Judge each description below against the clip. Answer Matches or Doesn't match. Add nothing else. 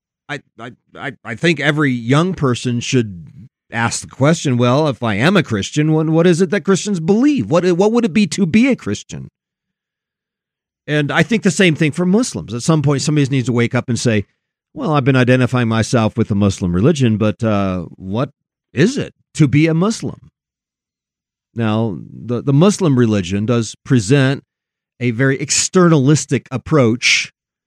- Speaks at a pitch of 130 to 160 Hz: Matches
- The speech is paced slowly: Doesn't match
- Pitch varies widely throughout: Matches